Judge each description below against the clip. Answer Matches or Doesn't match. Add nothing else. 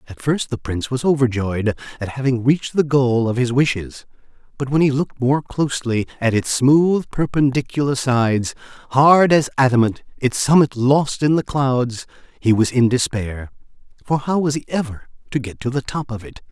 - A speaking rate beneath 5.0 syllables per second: Doesn't match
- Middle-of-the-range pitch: Doesn't match